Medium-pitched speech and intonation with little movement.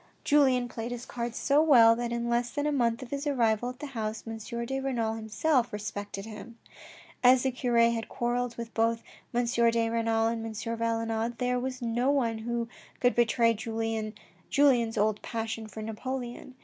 No: high, 235 Hz; narrow, 1.7 semitones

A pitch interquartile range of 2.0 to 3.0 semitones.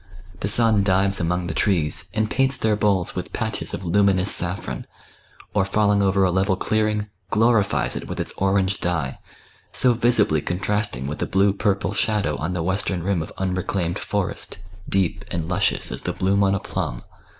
Yes: narrow, 2.6 semitones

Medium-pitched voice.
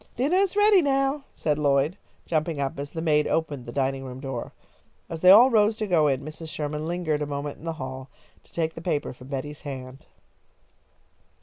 Yes: medium, 150 Hz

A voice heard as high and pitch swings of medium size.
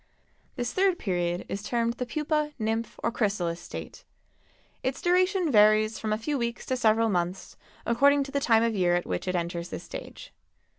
No: high, 225 Hz; wide, 6.0 semitones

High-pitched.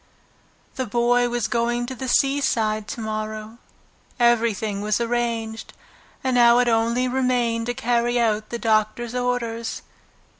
Yes: high, 235 Hz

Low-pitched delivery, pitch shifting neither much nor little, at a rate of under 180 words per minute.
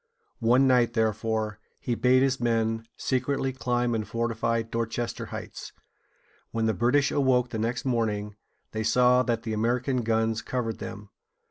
No: low, 115 Hz; narrow, 1.9 semitones; average, 150 wpm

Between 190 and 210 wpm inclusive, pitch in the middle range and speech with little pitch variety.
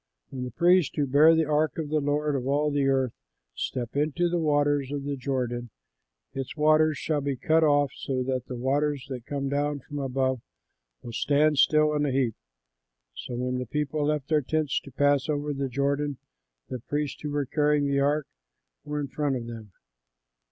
Yes: average, 195 wpm; medium, 145 Hz; narrow, 2.1 semitones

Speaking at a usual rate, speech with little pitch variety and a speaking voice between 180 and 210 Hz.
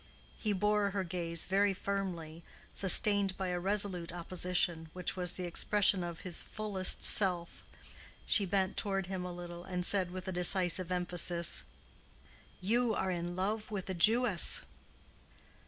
Yes: average, 145 wpm; narrow, 2.2 semitones; medium, 185 Hz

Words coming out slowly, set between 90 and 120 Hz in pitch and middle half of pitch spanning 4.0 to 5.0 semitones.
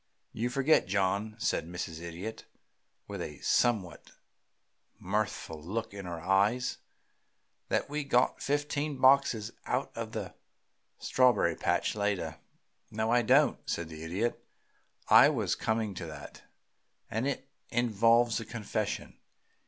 Yes: slow, 125 wpm; low, 110 Hz; average, 4.5 semitones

